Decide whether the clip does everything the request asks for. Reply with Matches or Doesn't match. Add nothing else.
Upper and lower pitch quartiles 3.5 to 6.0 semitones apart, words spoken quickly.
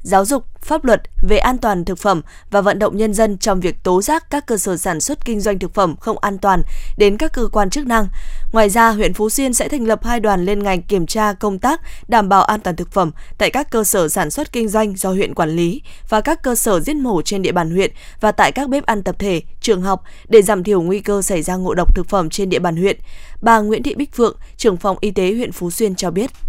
Doesn't match